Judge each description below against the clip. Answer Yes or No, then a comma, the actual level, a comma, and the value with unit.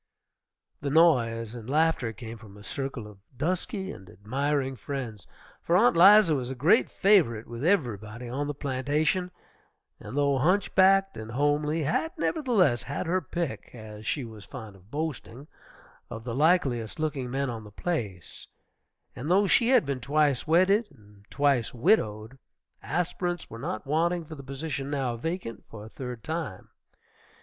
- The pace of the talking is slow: No, average, 160 wpm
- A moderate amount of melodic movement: No, wide, 6.3 semitones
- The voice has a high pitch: No, medium, 140 Hz